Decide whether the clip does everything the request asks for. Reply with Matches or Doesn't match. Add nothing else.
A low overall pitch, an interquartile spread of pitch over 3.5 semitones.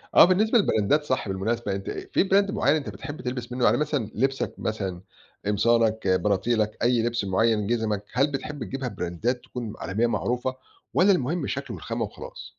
Matches